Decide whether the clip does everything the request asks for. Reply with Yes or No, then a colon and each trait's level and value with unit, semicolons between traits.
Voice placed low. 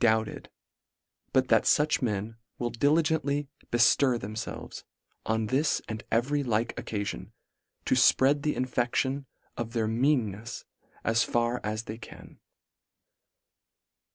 Yes: low, 120 Hz